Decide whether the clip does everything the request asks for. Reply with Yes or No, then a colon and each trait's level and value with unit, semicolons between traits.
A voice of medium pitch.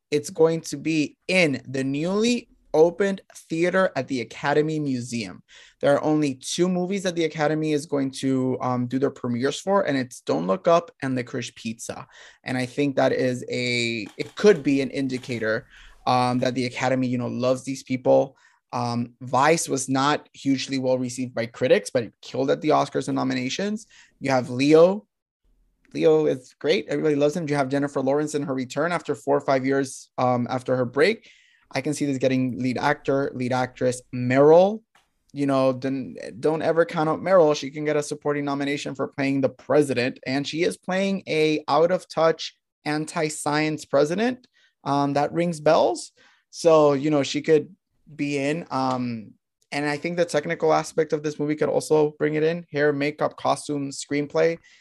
Yes: medium, 145 Hz